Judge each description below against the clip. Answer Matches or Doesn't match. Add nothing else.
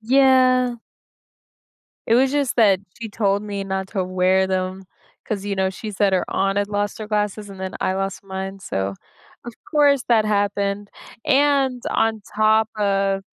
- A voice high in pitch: Matches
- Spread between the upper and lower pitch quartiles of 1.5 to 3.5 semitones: Matches